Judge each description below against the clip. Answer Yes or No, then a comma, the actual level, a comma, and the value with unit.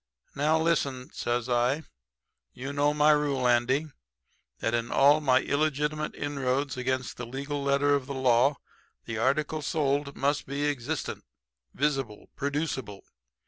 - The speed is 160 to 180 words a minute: No, slow, 135 wpm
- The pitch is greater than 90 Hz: Yes, medium, 140 Hz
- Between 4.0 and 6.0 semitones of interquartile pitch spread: No, narrow, 2.4 semitones